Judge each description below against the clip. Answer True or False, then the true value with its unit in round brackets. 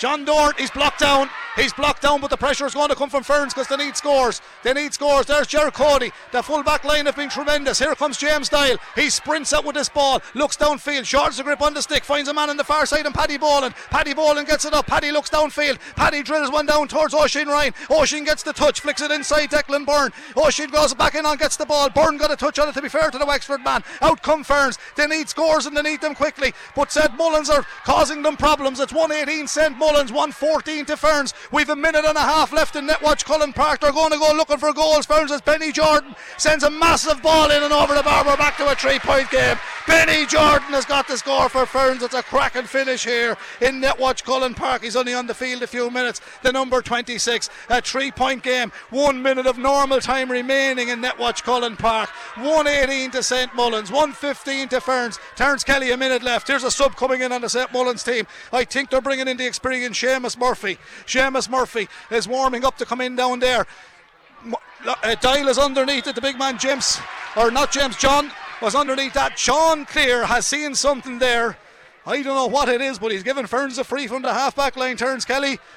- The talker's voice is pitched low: False (280 Hz)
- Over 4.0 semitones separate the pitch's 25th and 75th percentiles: False (2.6 semitones)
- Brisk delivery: True (230 wpm)